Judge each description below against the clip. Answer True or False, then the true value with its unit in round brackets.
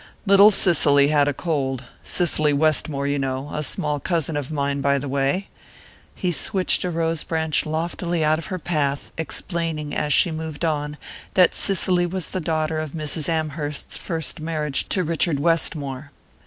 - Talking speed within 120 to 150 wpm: False (170 wpm)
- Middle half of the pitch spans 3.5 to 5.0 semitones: False (2.6 semitones)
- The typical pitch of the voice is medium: True (155 Hz)